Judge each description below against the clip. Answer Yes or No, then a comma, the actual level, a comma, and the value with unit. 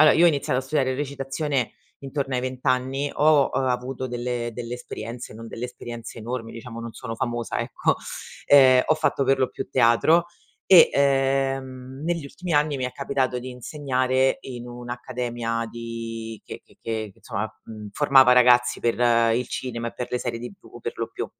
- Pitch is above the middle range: No, low, 125 Hz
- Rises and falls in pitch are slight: Yes, narrow, 2.3 semitones